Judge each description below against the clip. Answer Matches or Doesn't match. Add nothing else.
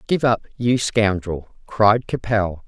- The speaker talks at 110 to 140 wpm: Matches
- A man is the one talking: Doesn't match